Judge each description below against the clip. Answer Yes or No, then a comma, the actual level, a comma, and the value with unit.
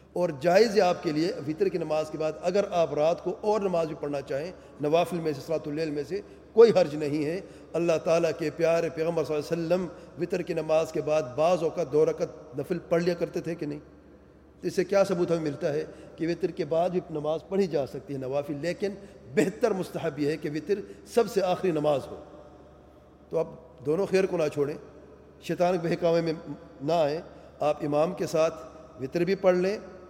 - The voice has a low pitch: No, medium, 165 Hz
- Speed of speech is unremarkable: No, fast, 215 wpm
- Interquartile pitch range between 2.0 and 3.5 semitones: Yes, narrow, 2.6 semitones